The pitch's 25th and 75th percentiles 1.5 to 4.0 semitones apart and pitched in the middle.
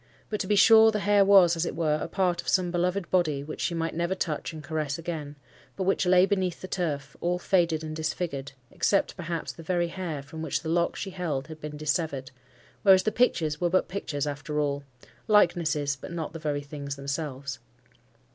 Yes: average, 3.6 semitones; medium, 165 Hz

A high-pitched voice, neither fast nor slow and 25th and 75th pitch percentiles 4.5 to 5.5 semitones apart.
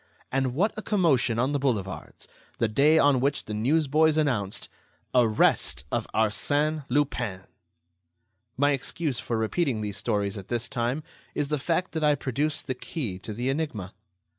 No: low, 130 Hz; average, 160 wpm; average, 5.2 semitones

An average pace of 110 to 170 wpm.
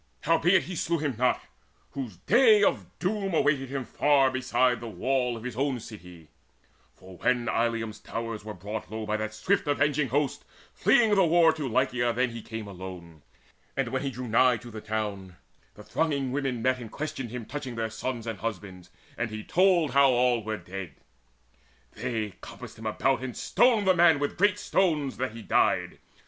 No: average, 185 wpm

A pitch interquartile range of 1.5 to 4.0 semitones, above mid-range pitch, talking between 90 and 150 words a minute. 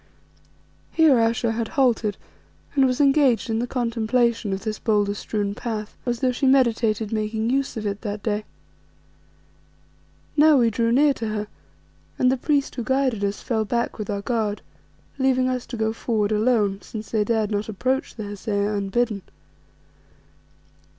No: average, 3.0 semitones; high, 225 Hz; average, 160 wpm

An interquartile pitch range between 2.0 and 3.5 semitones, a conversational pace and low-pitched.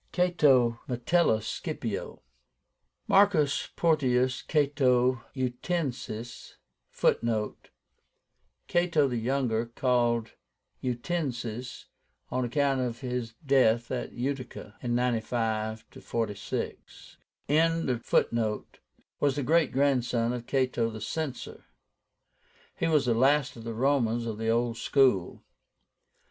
No: average, 3.2 semitones; slow, 95 wpm; low, 125 Hz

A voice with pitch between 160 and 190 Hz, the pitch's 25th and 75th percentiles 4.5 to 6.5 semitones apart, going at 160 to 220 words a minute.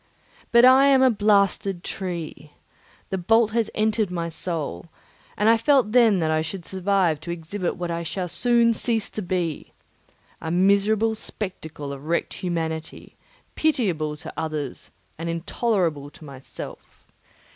No: medium, 185 Hz; average, 5.1 semitones; average, 140 wpm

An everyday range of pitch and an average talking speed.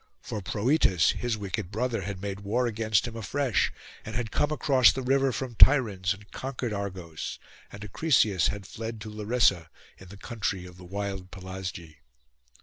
Yes: average, 4.2 semitones; average, 165 wpm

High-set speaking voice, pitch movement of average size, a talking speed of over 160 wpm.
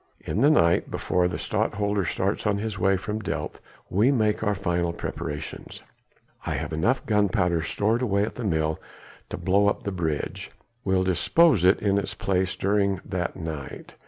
No: very low, 95 Hz; average, 3.0 semitones; average, 170 wpm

